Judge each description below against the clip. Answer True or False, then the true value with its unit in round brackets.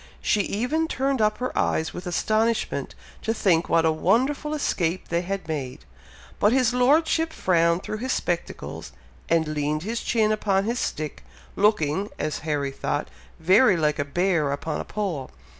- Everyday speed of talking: True (160 wpm)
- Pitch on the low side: False (190 Hz)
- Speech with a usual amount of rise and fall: False (6.4 semitones)